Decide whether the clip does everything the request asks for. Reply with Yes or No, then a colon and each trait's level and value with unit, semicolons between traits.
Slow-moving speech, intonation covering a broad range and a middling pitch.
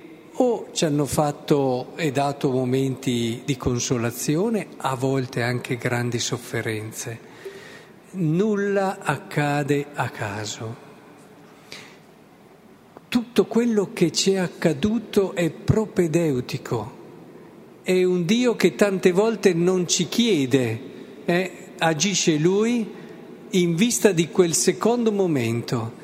Yes: slow, 100 wpm; wide, 7.1 semitones; medium, 170 Hz